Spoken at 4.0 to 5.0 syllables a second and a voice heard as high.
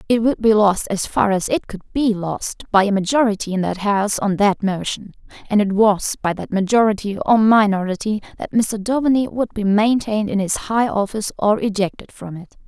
No: 5.3 syllables/s; high, 210 Hz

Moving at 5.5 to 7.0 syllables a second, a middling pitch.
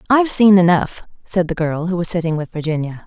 Yes: 6.0 syllables/s; medium, 175 Hz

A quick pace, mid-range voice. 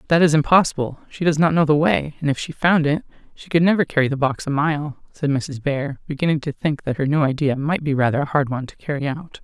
Yes: fast, 260 wpm; medium, 150 Hz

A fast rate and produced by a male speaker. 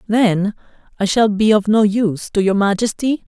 No: average, 180 wpm; male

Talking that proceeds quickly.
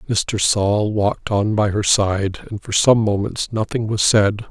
No: average, 185 wpm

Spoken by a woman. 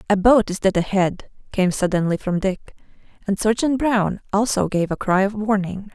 Yes: female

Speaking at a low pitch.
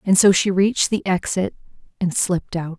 No: medium, 185 Hz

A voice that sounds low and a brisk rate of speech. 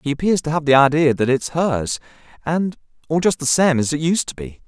No: medium, 150 Hz; fast, 255 wpm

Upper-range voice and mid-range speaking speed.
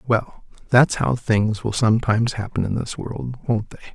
No: low, 115 Hz; average, 180 wpm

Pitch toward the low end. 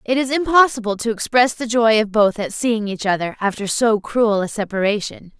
No: high, 225 Hz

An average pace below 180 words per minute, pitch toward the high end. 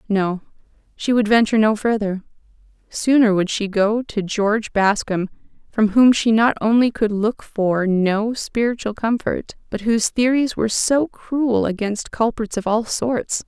Yes: average, 150 wpm; high, 220 Hz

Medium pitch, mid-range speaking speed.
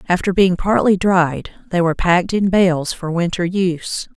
Yes: medium, 180 Hz; average, 170 wpm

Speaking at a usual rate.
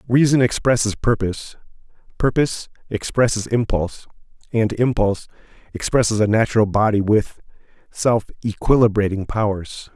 No: slow, 95 wpm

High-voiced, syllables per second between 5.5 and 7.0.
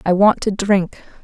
No: high, 195 Hz; 4.1 syllables/s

